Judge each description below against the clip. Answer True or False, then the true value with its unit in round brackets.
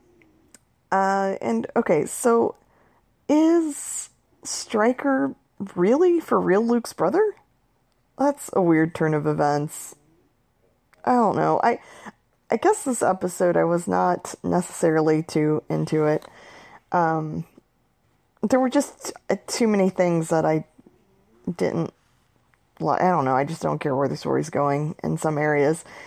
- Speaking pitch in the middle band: True (175 Hz)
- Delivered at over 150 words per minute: False (135 wpm)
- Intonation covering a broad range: True (7.4 semitones)